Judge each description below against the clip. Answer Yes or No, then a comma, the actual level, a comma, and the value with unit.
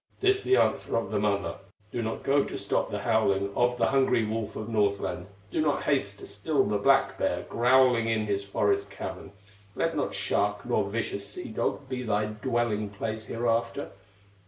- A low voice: Yes, low, 110 Hz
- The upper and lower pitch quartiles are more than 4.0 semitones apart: No, average, 3.2 semitones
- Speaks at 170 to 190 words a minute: Yes, average, 180 wpm